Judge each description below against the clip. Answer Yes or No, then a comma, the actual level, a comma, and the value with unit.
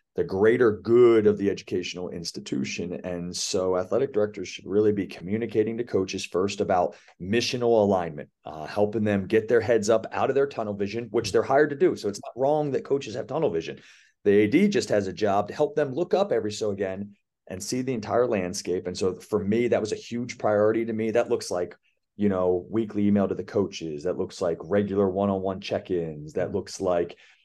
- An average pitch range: Yes, average, 3.4 semitones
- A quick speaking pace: Yes, fast, 215 wpm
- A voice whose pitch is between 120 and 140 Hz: No, low, 105 Hz